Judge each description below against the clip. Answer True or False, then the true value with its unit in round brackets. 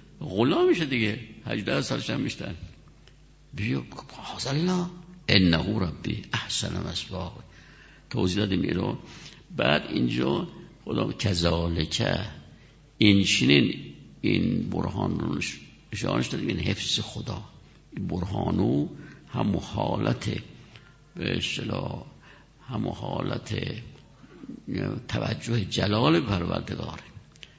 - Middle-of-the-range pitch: False (105 Hz)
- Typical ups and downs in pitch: True (5.0 semitones)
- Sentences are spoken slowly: True (85 wpm)